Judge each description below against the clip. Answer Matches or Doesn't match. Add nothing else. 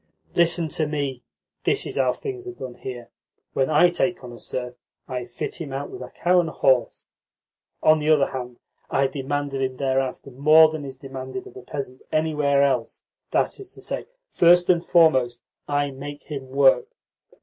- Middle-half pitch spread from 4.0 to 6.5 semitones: Doesn't match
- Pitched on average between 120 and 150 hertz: Matches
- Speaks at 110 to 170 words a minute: Doesn't match